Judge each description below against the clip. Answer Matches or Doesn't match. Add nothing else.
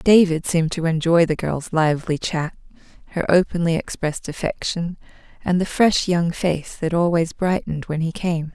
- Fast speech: Doesn't match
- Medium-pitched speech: Matches